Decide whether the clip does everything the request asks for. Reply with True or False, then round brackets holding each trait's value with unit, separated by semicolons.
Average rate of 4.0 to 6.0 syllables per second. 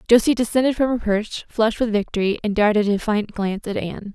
False (6.4 syllables/s)